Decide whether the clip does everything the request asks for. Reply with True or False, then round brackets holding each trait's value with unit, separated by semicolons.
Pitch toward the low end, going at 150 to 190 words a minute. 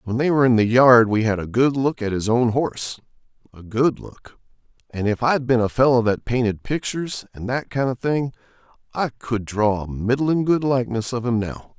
False (120 Hz; 205 wpm)